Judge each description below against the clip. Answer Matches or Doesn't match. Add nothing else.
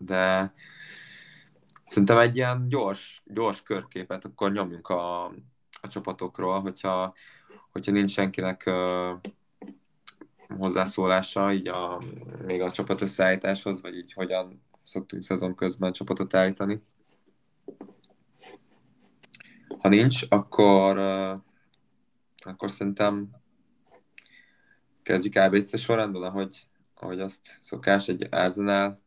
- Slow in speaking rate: Matches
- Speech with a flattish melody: Matches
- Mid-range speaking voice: Doesn't match